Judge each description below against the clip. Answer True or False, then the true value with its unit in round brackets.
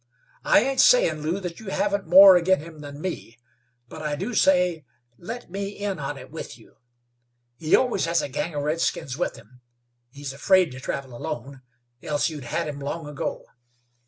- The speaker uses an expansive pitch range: False (4.9 semitones)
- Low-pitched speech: False (160 Hz)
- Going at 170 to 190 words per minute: True (185 wpm)